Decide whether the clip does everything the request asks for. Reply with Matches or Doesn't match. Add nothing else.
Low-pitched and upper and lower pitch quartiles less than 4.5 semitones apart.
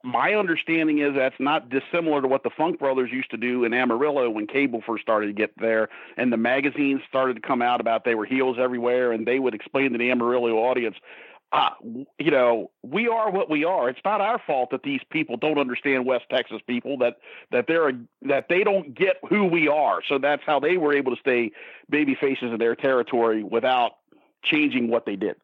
Matches